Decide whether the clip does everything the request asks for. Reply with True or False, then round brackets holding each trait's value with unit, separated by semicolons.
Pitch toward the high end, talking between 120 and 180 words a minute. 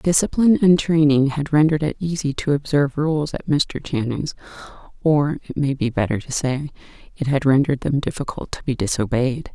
False (145 Hz; 175 wpm)